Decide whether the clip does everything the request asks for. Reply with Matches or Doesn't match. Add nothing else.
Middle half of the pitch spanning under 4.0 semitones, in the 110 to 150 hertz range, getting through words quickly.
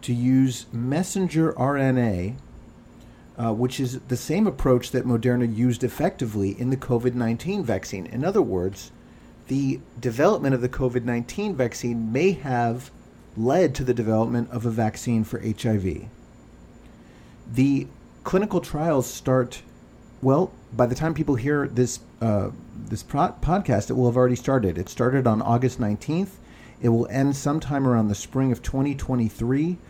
Doesn't match